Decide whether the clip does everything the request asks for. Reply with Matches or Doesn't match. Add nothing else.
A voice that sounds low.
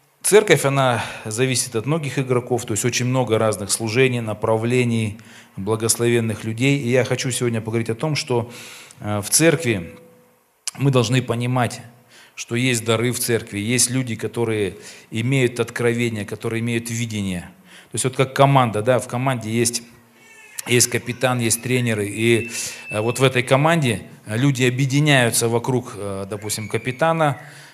Matches